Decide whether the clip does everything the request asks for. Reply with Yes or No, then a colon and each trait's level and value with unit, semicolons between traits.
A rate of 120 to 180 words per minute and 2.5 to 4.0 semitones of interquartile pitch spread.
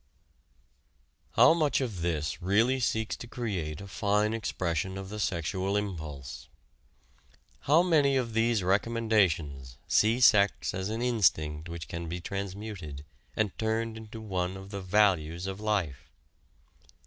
No: slow, 135 wpm; average, 4.5 semitones